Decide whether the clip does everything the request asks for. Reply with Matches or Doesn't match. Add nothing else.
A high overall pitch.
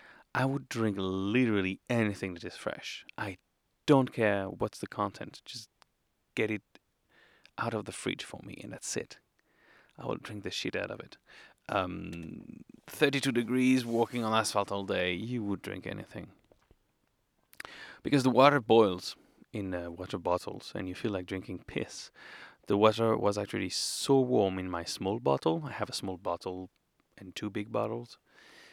Doesn't match